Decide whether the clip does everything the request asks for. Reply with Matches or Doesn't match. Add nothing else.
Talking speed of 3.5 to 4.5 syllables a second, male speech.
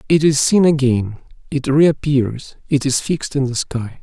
Matches